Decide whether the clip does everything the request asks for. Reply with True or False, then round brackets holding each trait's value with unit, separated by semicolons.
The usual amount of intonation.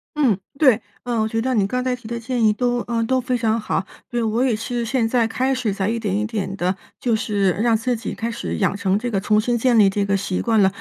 True (3.0 semitones)